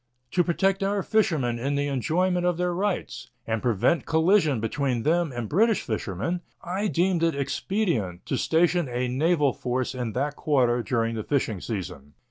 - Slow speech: No, average, 165 wpm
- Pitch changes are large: Yes, wide, 6.6 semitones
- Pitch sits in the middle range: Yes, medium, 145 Hz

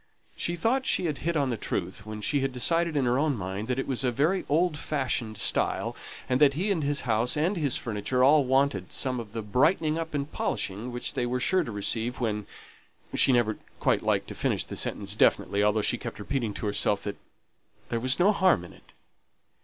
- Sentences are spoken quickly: Yes, fast, 215 wpm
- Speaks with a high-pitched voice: No, low, 130 Hz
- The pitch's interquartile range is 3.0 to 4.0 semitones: No, wide, 5.5 semitones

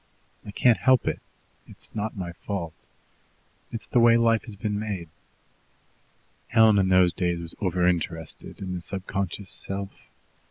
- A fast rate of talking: No, average, 150 wpm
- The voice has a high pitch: No, very low, 95 Hz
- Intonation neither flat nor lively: Yes, average, 3.6 semitones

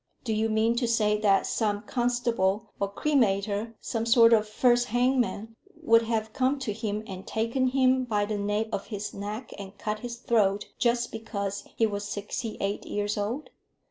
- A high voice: Yes, high, 220 Hz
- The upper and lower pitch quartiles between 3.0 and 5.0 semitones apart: No, narrow, 2.6 semitones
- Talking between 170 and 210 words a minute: Yes, average, 175 wpm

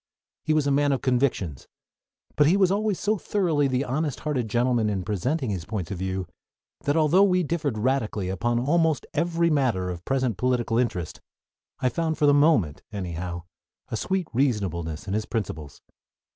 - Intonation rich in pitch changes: Yes, wide, 7.6 semitones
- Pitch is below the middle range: Yes, low, 125 Hz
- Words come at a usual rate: Yes, average, 170 wpm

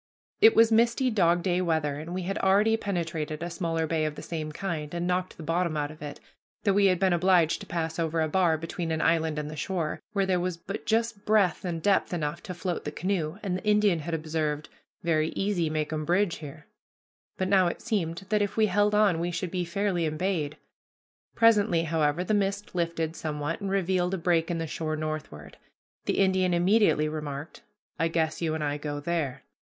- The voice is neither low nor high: Yes, medium, 170 Hz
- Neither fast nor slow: No, fast, 210 wpm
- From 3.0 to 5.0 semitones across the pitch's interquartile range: Yes, average, 3.5 semitones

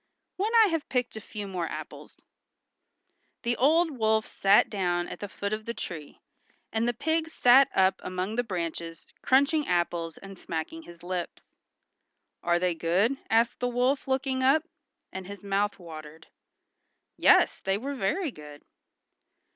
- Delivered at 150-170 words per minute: Yes, average, 155 wpm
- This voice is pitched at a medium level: No, high, 205 Hz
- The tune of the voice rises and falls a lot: Yes, wide, 7.0 semitones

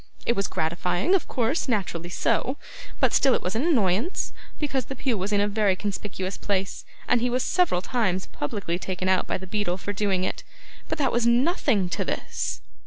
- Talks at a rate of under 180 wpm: No, average, 195 wpm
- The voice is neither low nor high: No, high, 205 Hz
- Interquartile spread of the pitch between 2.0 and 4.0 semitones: No, average, 5.0 semitones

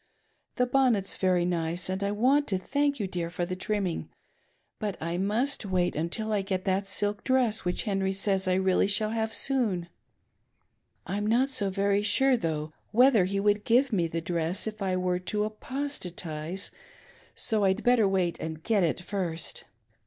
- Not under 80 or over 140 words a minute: No, average, 175 wpm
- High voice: Yes, high, 195 Hz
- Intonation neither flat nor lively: Yes, average, 3.4 semitones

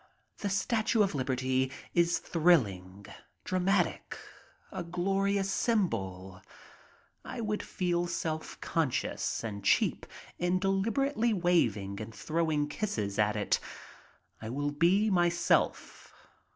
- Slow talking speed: Yes, slow, 110 wpm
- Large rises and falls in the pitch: Yes, wide, 8.7 semitones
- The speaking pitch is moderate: Yes, medium, 170 Hz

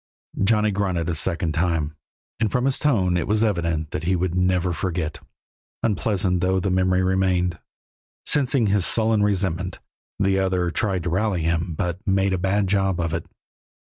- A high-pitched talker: No, very low, 95 Hz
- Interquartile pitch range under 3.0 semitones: Yes, narrow, 2.4 semitones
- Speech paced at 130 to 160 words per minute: No, average, 170 wpm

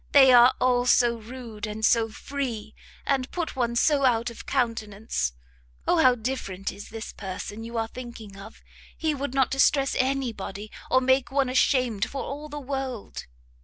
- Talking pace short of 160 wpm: No, average, 165 wpm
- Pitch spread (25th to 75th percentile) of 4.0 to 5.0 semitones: No, average, 3.2 semitones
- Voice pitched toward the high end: Yes, high, 245 Hz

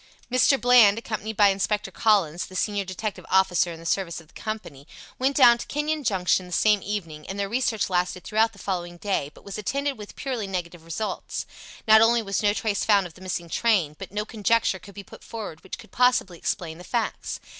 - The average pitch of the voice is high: Yes, high, 200 Hz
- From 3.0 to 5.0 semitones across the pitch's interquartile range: Yes, average, 3.7 semitones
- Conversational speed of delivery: No, fast, 210 wpm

